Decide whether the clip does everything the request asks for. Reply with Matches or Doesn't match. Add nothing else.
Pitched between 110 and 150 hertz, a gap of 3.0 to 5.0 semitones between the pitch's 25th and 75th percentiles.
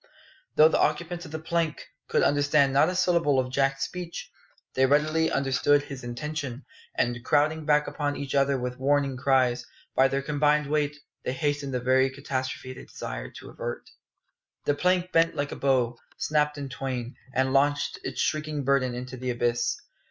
Doesn't match